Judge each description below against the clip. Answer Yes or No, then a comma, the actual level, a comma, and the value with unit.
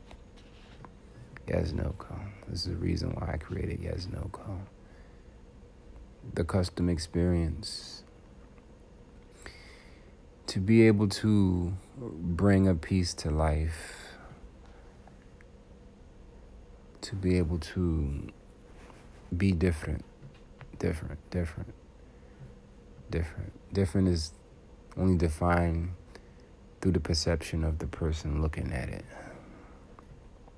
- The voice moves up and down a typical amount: Yes, average, 3.2 semitones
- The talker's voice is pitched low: Yes, very low, 90 Hz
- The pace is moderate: No, slow, 90 wpm